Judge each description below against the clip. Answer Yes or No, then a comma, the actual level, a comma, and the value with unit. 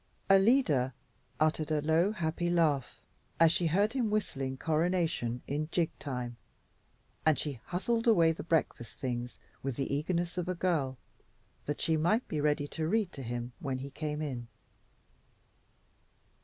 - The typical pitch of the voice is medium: Yes, medium, 155 Hz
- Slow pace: No, average, 150 wpm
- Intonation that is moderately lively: Yes, average, 4.4 semitones